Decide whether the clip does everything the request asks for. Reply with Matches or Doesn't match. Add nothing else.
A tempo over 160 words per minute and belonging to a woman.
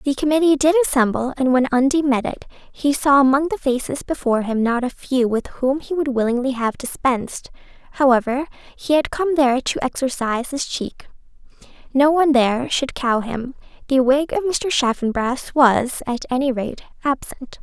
Matches